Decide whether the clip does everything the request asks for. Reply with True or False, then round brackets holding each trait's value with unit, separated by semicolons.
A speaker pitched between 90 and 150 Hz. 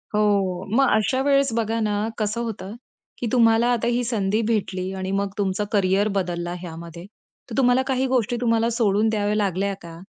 False (210 Hz)